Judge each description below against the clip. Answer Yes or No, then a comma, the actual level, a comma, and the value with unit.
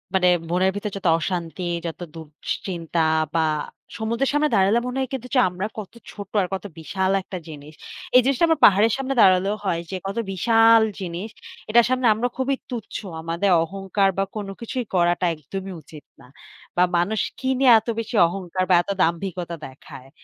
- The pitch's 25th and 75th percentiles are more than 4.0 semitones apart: Yes, average, 4.5 semitones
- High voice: Yes, high, 195 Hz